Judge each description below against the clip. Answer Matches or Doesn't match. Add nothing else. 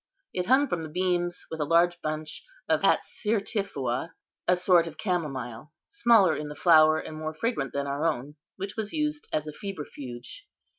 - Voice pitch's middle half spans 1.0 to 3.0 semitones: Doesn't match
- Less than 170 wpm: Doesn't match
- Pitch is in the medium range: Matches